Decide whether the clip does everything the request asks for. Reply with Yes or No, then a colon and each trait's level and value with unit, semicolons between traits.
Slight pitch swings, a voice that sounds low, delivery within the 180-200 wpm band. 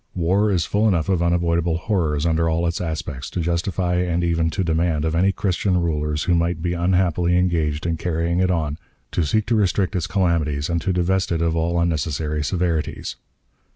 Yes: narrow, 1.9 semitones; very low, 85 Hz; average, 190 wpm